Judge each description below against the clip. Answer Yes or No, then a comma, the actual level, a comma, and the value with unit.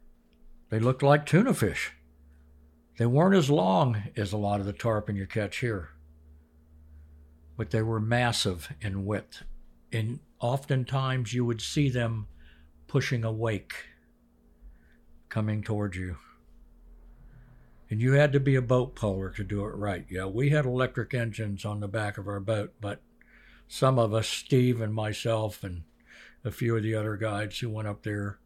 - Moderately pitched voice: No, low, 105 Hz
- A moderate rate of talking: Yes, average, 160 wpm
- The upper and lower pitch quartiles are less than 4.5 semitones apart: No, wide, 5.6 semitones